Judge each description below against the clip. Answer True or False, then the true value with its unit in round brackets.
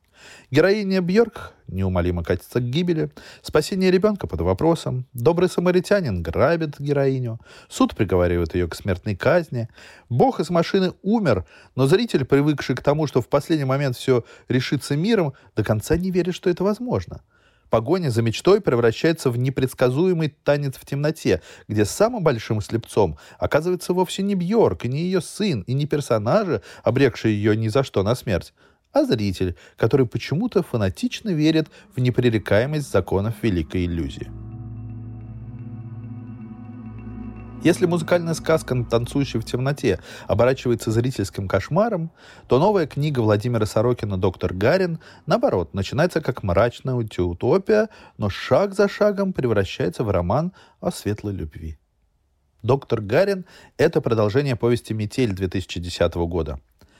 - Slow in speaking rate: False (130 wpm)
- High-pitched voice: False (125 Hz)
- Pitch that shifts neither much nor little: False (7.0 semitones)